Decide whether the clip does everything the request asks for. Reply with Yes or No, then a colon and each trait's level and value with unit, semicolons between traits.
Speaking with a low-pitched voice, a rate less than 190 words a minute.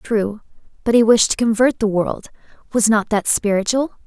No: high, 220 Hz; average, 175 wpm